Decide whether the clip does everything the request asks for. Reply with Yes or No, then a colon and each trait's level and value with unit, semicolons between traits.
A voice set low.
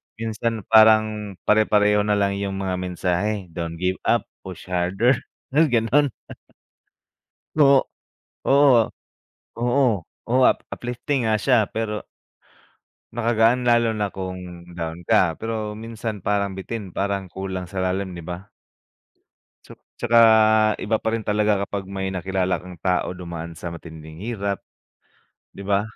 Yes: low, 100 Hz